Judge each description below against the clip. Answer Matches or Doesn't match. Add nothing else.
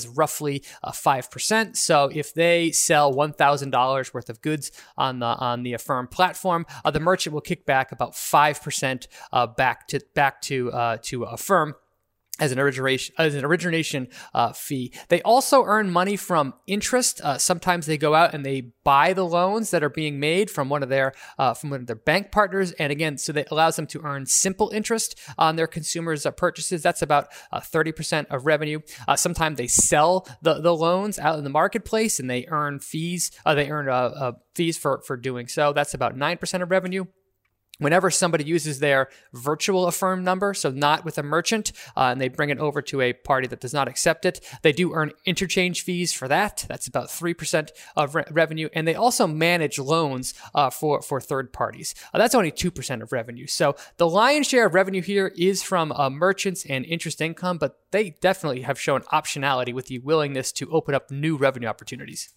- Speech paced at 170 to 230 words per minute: Matches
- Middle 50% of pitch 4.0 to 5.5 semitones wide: Matches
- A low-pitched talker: Doesn't match